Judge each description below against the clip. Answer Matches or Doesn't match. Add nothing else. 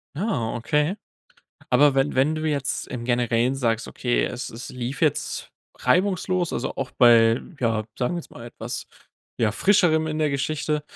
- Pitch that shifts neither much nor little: Matches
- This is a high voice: Doesn't match